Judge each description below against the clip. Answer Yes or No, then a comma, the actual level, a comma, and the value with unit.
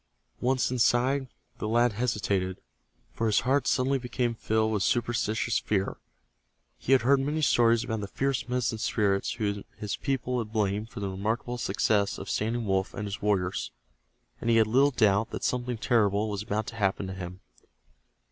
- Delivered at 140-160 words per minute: No, average, 170 wpm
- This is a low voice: Yes, low, 110 Hz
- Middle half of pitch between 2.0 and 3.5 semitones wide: Yes, average, 3.2 semitones